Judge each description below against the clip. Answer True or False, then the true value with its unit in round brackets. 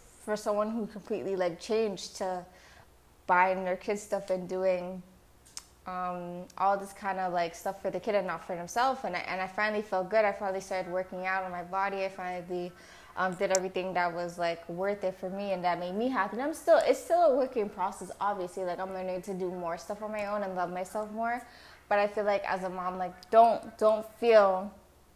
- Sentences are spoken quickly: True (220 wpm)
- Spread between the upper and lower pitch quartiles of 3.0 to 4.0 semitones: False (2.5 semitones)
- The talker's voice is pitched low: False (190 Hz)